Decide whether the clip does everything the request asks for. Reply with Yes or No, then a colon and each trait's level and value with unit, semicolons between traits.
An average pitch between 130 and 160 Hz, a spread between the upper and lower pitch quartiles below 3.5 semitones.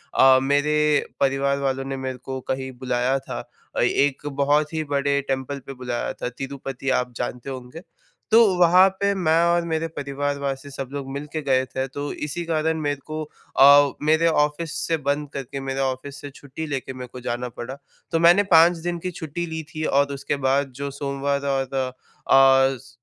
Yes: medium, 140 Hz; narrow, 2.4 semitones